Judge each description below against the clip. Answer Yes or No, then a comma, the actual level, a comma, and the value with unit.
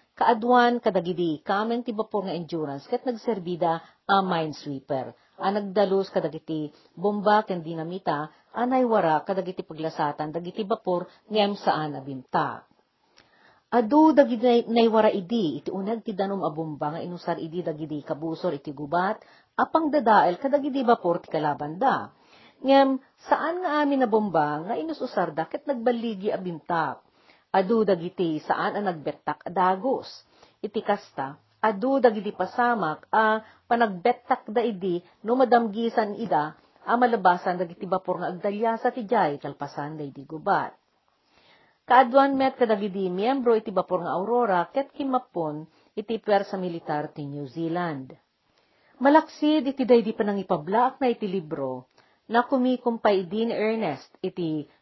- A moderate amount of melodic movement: No, wide, 6.4 semitones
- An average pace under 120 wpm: No, average, 130 wpm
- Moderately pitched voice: No, high, 200 Hz